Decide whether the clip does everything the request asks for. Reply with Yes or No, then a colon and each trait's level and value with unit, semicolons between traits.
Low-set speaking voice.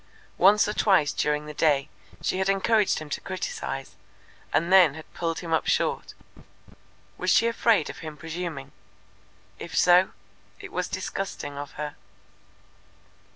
No: medium, 175 Hz